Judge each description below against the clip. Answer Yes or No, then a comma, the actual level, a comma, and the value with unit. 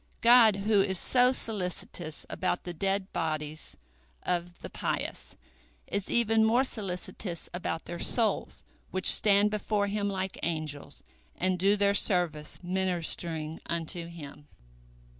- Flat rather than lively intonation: No, average, 3.2 semitones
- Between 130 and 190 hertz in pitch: Yes, medium, 185 Hz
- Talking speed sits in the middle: No, slow, 130 wpm